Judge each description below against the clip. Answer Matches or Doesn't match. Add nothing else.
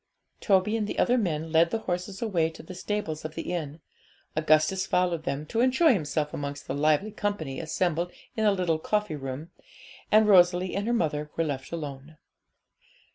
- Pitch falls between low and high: Matches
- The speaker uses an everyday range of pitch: Matches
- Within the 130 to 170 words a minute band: Doesn't match